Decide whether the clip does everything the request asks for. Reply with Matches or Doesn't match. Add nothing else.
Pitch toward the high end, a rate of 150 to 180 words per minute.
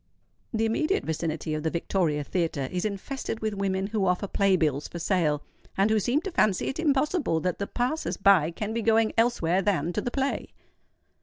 Doesn't match